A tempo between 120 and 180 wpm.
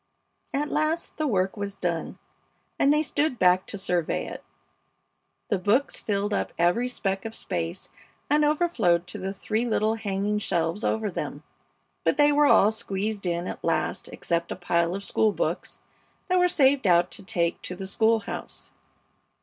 Yes: average, 170 wpm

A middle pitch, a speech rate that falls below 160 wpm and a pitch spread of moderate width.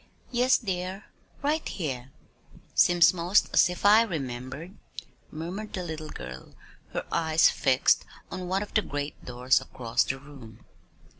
No: medium, 165 Hz; average, 140 wpm; wide, 6.2 semitones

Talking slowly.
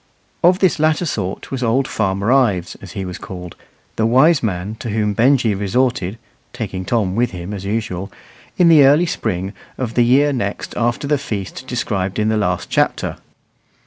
No: average, 175 wpm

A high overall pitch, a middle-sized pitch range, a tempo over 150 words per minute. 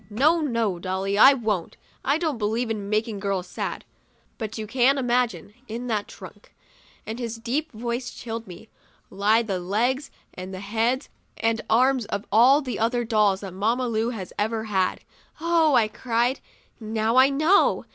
Yes: high, 225 Hz; average, 3.3 semitones; average, 165 wpm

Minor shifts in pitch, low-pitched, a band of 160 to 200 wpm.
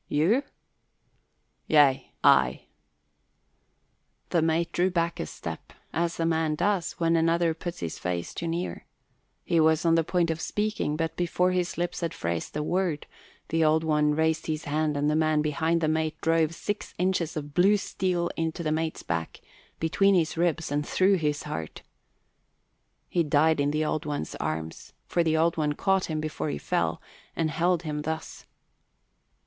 No: narrow, 2.1 semitones; medium, 160 Hz; average, 170 wpm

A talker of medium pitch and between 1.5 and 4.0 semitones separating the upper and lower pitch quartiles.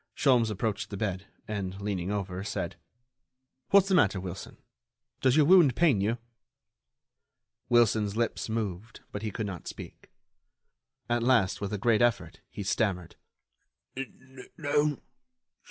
No: low, 110 Hz; average, 3.7 semitones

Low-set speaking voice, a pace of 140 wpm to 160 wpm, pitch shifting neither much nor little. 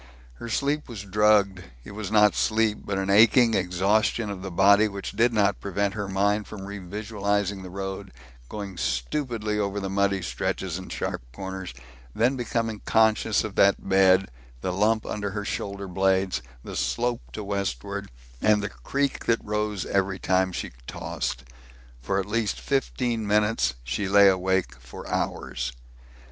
No: low, 100 Hz; average, 155 wpm; narrow, 2.0 semitones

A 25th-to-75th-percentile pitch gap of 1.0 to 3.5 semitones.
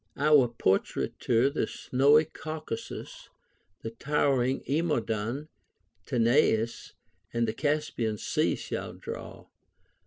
No: average, 4.6 semitones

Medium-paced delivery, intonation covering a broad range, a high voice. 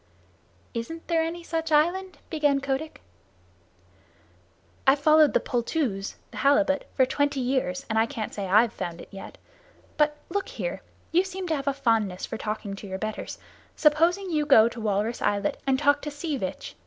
Yes: average, 175 wpm; wide, 6.1 semitones; very high, 275 Hz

